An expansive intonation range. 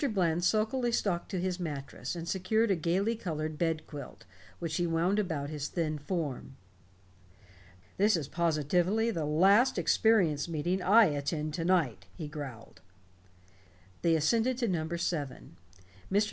No: average, 4.1 semitones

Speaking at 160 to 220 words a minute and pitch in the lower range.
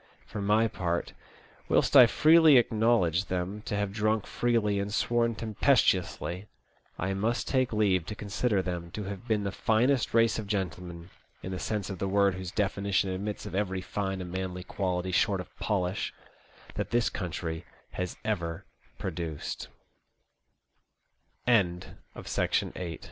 No: slow, 135 wpm; low, 100 Hz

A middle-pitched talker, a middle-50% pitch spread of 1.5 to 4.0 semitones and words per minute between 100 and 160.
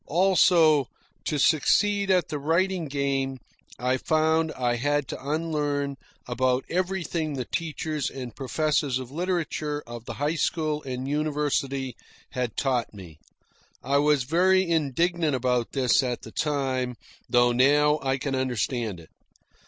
Yes: medium, 145 Hz; average, 3.6 semitones; slow, 135 wpm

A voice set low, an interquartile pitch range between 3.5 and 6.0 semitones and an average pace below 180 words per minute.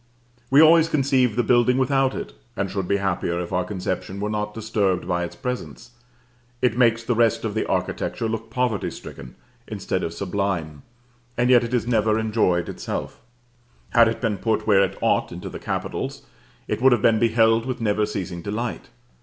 No: low, 110 Hz; average, 3.8 semitones; average, 185 wpm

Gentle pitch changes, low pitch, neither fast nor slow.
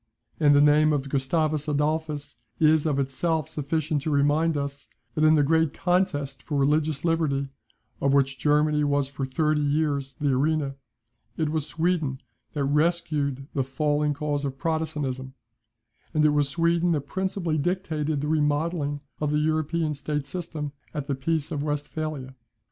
No: narrow, 1.9 semitones; medium, 150 Hz; average, 155 wpm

